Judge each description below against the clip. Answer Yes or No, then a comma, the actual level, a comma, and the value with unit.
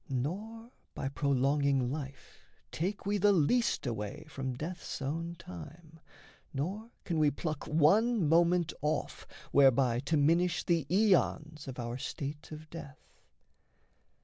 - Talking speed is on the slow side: Yes, slow, 125 wpm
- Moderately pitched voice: Yes, medium, 155 Hz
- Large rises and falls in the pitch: No, average, 4.0 semitones